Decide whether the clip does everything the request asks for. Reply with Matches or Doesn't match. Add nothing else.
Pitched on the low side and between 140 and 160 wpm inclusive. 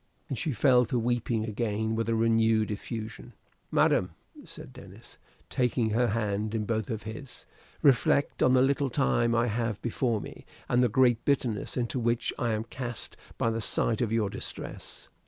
Doesn't match